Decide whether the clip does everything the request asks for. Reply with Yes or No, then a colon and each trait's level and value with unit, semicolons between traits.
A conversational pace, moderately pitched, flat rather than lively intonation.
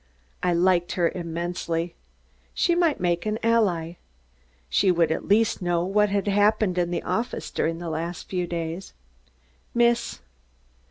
No: average, 145 wpm; medium, 180 Hz; average, 3.5 semitones